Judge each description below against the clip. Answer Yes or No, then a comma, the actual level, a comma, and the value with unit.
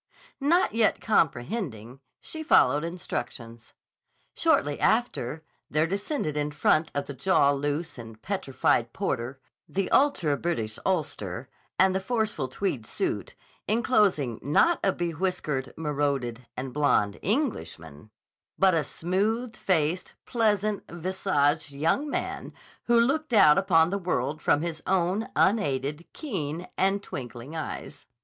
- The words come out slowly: Yes, slow, 125 wpm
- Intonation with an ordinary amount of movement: No, wide, 6.2 semitones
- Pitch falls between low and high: Yes, medium, 160 Hz